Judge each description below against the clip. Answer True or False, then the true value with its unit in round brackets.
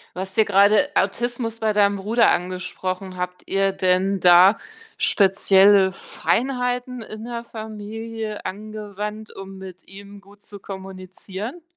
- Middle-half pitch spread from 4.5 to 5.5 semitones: False (2.4 semitones)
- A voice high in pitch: True (200 Hz)